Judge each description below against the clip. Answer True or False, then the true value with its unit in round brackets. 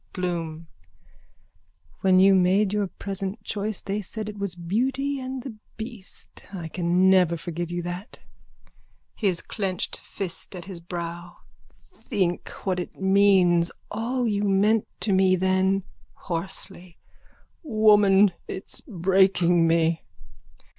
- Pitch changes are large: False (2.9 semitones)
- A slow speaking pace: True (125 wpm)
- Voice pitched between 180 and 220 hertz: True (190 Hz)